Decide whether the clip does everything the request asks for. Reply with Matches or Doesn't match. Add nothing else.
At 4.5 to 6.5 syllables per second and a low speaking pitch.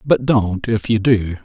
Doesn't match